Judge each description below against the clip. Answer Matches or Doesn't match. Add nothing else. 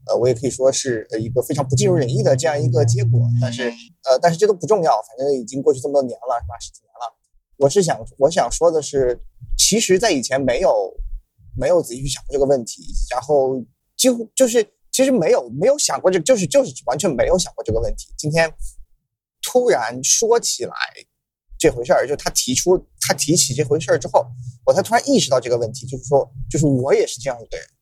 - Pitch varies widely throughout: Matches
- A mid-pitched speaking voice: Matches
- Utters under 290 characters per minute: Doesn't match